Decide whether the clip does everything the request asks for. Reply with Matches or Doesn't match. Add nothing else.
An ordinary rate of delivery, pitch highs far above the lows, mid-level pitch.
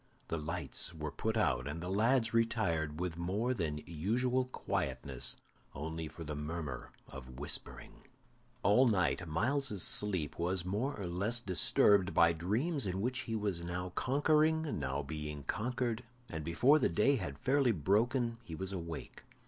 Doesn't match